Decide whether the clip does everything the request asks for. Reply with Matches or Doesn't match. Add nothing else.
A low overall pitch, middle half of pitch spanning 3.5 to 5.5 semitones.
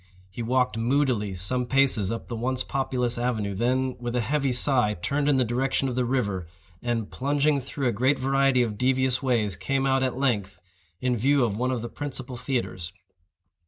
Doesn't match